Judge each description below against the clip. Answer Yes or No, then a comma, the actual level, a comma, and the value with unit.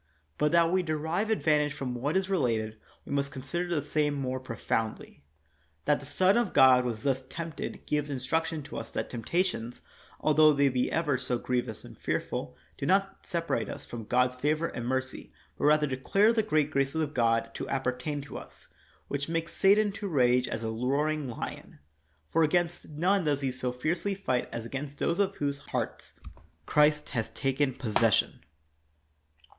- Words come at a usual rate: Yes, average, 180 wpm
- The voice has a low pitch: No, medium, 145 Hz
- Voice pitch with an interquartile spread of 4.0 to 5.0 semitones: Yes, average, 4.5 semitones